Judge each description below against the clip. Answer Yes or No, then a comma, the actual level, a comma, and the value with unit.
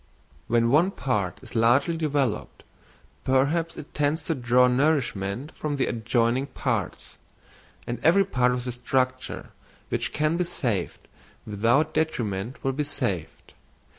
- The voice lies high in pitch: No, low, 130 Hz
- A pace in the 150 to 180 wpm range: No, slow, 135 wpm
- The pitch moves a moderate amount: Yes, average, 4.3 semitones